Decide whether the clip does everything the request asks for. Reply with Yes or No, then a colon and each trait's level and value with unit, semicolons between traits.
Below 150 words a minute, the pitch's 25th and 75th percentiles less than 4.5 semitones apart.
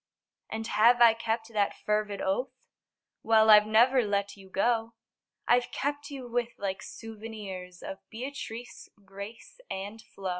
Yes: average, 140 wpm; average, 2.8 semitones